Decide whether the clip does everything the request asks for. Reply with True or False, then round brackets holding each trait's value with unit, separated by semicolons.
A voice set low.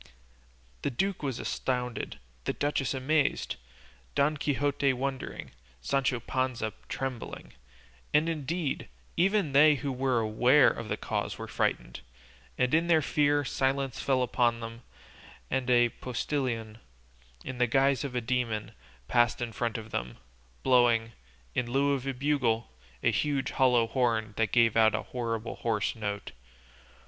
True (125 Hz)